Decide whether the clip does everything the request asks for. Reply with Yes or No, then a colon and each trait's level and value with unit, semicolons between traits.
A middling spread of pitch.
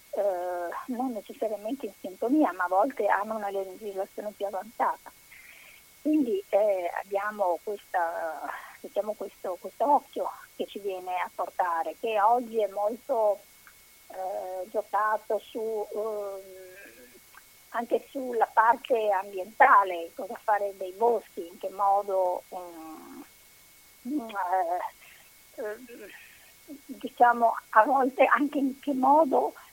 Yes: average, 4.8 semitones